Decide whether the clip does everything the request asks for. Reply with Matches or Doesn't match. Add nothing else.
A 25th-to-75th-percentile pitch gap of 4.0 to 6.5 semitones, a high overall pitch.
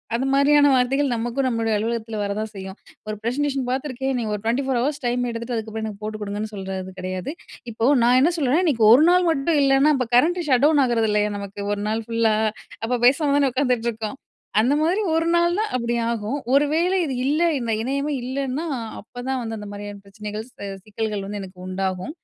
Matches